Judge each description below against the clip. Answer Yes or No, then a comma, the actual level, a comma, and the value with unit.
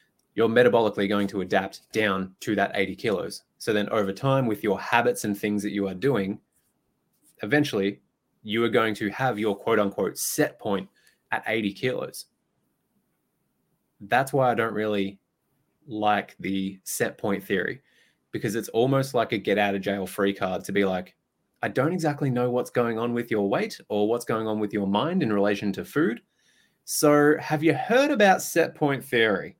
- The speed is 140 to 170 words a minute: No, average, 180 wpm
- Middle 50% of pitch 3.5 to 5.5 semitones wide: Yes, average, 4.1 semitones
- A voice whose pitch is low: Yes, low, 105 Hz